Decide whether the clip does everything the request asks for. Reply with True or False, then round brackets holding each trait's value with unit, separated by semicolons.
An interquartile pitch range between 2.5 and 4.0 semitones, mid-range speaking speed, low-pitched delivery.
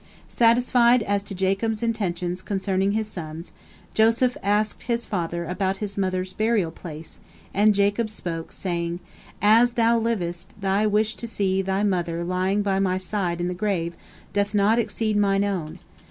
False (2.9 semitones; 155 wpm; 200 Hz)